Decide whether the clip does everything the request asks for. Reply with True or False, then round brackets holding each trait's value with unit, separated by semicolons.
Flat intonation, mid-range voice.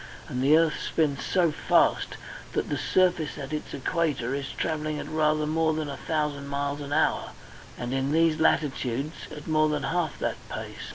True (2.0 semitones; 150 Hz)